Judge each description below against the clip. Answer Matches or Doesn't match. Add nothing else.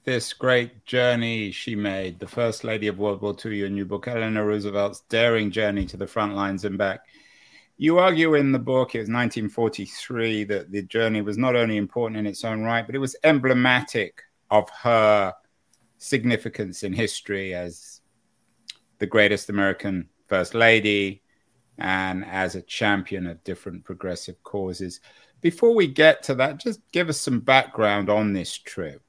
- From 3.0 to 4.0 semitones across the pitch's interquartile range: Matches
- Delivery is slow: Doesn't match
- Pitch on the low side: Matches